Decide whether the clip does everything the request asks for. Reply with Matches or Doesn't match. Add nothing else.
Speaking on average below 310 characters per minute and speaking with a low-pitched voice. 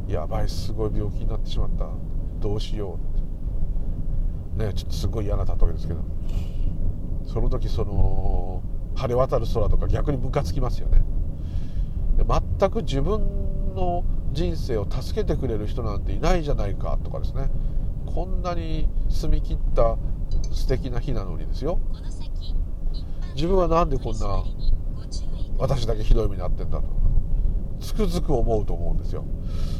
Matches